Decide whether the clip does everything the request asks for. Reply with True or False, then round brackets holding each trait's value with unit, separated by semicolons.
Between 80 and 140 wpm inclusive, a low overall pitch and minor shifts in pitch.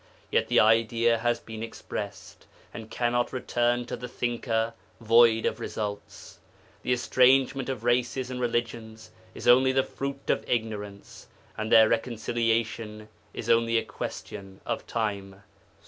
True (135 wpm; 115 Hz; 1.7 semitones)